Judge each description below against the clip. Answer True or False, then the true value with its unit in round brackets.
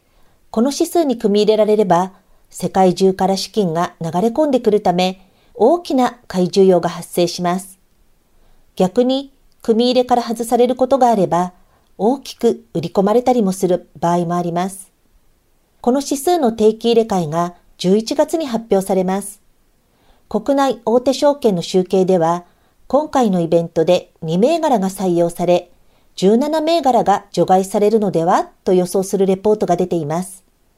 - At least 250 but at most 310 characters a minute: True (295 characters per minute)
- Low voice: False (200 Hz)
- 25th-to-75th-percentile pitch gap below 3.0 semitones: False (5.2 semitones)